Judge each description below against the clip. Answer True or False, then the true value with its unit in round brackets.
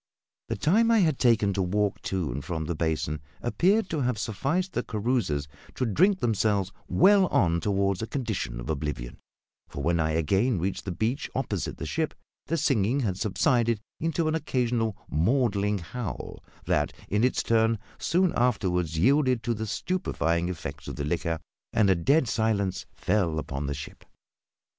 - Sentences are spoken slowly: False (165 wpm)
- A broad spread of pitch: True (6.6 semitones)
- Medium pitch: False (105 Hz)